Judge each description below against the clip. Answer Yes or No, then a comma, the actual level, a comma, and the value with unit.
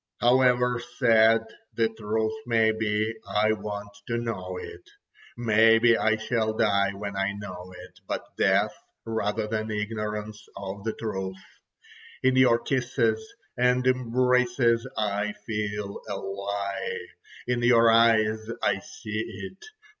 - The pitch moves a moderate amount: No, narrow, 2.1 semitones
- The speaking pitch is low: Yes, low, 110 Hz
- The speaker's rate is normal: No, slow, 125 wpm